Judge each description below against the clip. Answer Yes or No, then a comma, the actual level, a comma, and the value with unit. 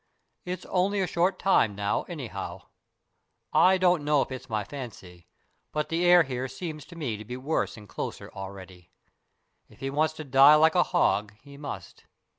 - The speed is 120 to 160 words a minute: No, average, 180 wpm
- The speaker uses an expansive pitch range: Yes, wide, 7.7 semitones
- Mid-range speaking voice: Yes, medium, 145 Hz